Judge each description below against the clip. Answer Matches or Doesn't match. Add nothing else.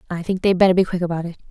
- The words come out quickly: Matches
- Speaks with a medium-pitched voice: Matches